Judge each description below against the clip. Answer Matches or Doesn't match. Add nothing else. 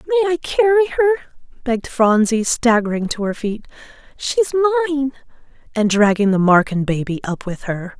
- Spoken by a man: Doesn't match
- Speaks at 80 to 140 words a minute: Matches